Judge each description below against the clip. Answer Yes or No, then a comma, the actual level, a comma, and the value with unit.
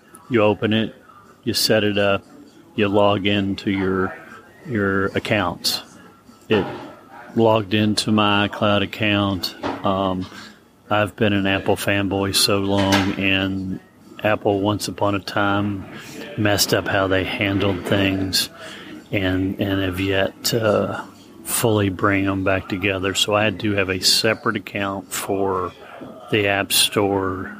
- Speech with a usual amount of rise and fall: No, narrow, 1.4 semitones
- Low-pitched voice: Yes, low, 100 Hz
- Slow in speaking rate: Yes, slow, 130 wpm